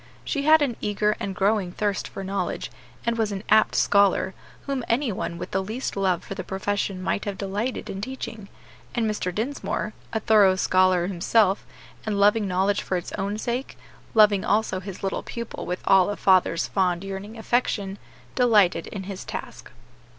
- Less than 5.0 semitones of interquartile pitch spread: Yes, narrow, 2.5 semitones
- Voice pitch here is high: Yes, high, 200 Hz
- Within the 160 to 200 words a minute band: Yes, average, 175 wpm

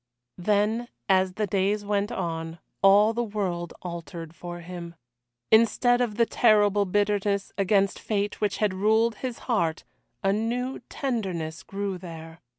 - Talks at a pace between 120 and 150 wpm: Yes, average, 140 wpm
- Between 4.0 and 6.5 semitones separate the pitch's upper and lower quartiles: No, average, 3.4 semitones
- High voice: Yes, high, 200 Hz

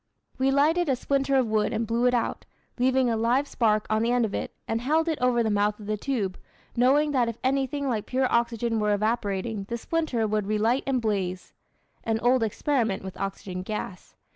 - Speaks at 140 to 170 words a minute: No, fast, 205 wpm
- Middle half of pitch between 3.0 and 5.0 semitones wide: Yes, average, 3.6 semitones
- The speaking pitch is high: Yes, high, 235 Hz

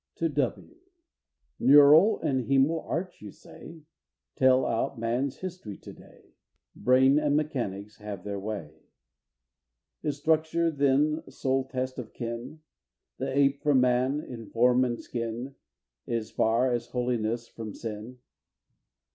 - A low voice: Yes, low, 130 Hz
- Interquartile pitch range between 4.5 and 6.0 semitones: No, average, 3.9 semitones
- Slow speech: Yes, slow, 130 wpm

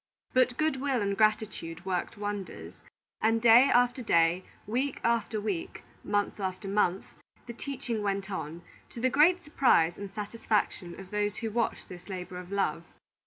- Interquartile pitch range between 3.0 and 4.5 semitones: Yes, average, 4.1 semitones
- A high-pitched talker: Yes, high, 210 Hz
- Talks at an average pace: Yes, average, 160 wpm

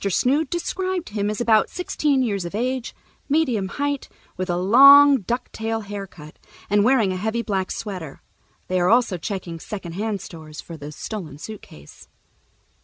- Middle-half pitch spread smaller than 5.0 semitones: No, wide, 5.5 semitones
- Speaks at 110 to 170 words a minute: Yes, average, 155 wpm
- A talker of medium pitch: No, high, 210 Hz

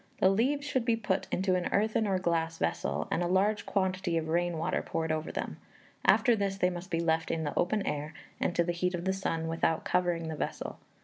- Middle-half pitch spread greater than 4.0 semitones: No, average, 3.0 semitones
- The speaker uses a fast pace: Yes, fast, 230 wpm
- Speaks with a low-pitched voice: No, medium, 180 Hz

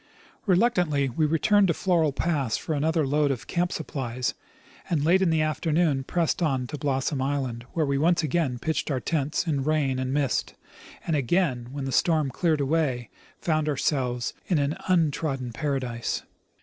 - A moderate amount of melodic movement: Yes, average, 3.5 semitones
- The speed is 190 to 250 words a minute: No, average, 165 wpm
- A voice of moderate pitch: Yes, medium, 150 Hz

